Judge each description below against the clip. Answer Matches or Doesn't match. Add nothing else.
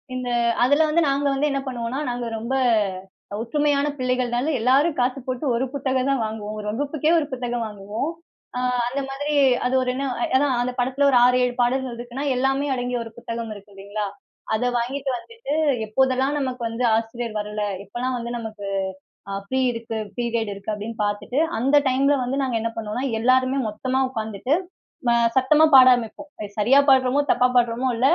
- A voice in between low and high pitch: Doesn't match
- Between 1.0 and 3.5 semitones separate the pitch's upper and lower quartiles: Matches